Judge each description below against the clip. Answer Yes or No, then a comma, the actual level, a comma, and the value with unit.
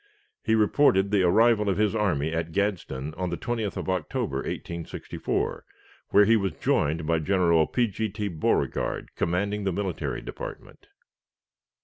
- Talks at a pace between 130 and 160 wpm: Yes, average, 145 wpm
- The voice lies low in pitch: Yes, very low, 95 Hz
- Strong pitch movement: No, average, 4.1 semitones